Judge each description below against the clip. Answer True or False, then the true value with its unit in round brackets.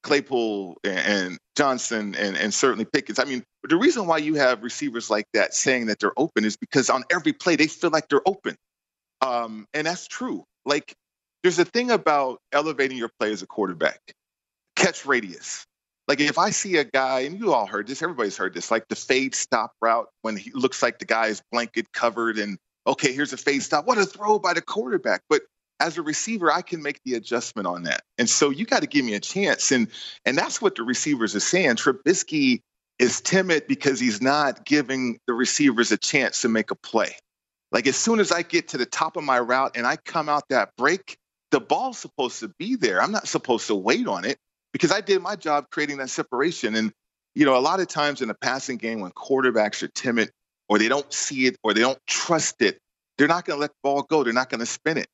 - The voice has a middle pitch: True (150 Hz)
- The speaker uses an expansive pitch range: True (6.8 semitones)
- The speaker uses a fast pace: True (225 wpm)